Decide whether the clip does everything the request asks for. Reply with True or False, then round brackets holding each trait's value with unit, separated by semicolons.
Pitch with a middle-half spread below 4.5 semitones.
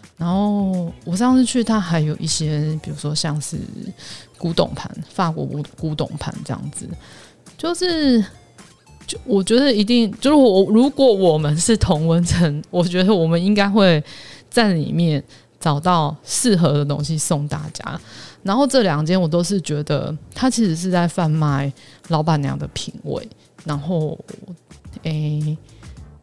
False (5.1 semitones)